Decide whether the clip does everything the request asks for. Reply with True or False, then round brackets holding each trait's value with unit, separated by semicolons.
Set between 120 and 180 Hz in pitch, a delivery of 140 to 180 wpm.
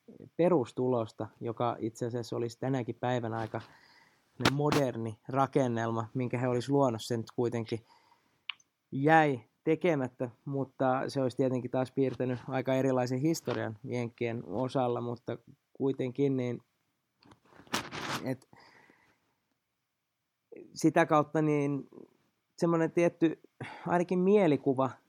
False (130 Hz; 95 wpm)